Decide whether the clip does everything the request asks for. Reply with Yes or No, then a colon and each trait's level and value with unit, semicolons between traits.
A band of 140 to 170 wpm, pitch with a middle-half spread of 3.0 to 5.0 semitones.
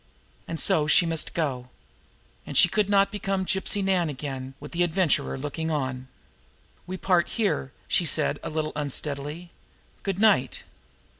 Yes: average, 150 wpm; average, 4.7 semitones